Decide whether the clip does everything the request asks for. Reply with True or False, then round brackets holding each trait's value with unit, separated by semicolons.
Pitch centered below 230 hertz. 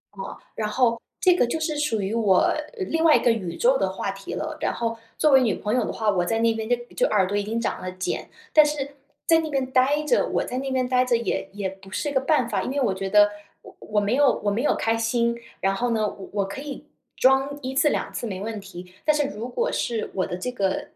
False (235 Hz)